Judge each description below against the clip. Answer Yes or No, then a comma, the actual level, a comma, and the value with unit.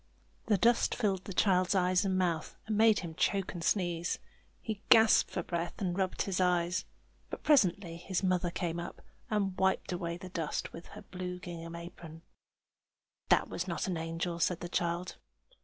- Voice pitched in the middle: Yes, medium, 180 Hz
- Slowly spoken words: No, average, 175 wpm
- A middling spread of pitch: No, narrow, 2.0 semitones